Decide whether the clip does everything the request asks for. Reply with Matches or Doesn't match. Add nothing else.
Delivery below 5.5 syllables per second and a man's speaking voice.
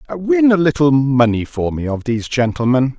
Matches